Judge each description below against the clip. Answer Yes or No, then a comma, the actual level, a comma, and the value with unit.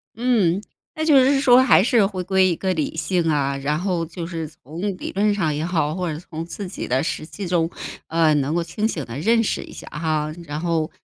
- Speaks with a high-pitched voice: No, medium, 170 Hz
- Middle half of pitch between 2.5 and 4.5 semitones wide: Yes, average, 4.2 semitones